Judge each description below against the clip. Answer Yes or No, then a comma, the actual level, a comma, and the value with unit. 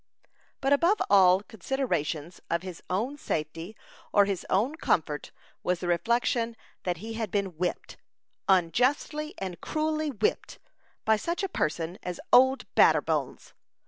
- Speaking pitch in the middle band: No, high, 205 Hz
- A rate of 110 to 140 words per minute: Yes, slow, 135 wpm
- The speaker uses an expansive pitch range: Yes, wide, 7.0 semitones